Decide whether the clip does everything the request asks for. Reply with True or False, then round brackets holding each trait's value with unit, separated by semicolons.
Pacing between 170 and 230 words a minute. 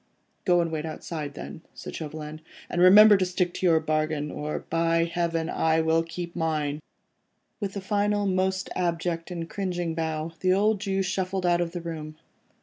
True (180 wpm)